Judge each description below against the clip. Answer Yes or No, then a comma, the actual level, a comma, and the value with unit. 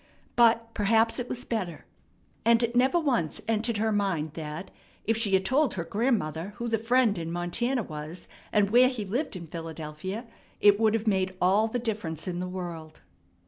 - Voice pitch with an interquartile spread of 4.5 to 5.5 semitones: Yes, average, 5.0 semitones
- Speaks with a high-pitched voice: Yes, high, 205 Hz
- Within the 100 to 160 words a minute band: No, average, 185 wpm